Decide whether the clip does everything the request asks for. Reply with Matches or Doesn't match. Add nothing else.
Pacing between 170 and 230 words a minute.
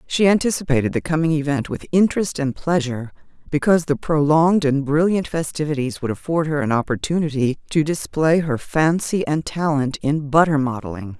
Doesn't match